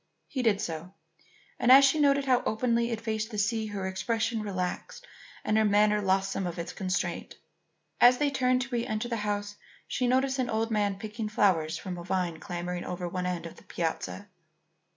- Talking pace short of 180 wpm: No, average, 195 wpm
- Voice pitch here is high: Yes, high, 210 Hz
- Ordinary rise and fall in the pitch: Yes, average, 4.2 semitones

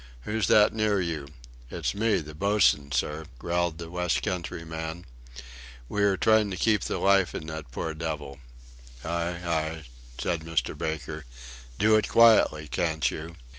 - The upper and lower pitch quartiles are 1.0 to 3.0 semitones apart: No, average, 3.9 semitones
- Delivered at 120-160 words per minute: Yes, average, 150 wpm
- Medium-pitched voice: No, very low, 85 Hz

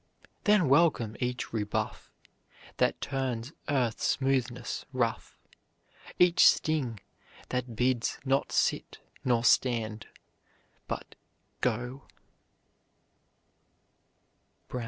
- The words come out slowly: Yes, slow, 75 wpm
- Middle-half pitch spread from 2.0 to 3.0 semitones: Yes, narrow, 2.6 semitones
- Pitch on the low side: Yes, low, 125 Hz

